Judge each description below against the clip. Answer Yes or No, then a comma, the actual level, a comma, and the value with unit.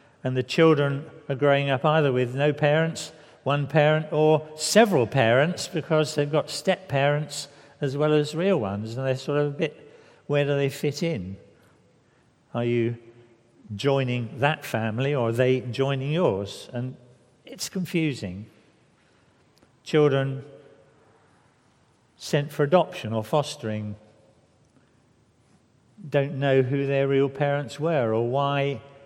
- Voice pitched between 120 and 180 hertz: Yes, medium, 140 Hz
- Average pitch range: Yes, average, 3.4 semitones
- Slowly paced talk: Yes, slow, 130 wpm